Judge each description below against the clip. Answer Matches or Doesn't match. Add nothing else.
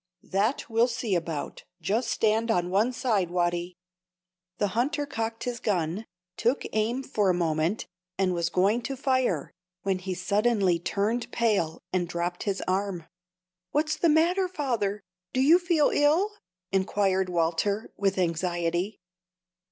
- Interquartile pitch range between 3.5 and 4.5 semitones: Doesn't match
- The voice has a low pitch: Doesn't match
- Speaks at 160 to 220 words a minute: Doesn't match